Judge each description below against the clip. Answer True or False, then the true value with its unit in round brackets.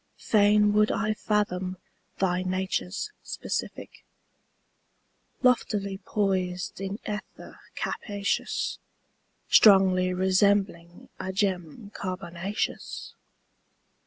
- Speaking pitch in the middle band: False (195 Hz)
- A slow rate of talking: True (75 wpm)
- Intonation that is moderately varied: False (2.1 semitones)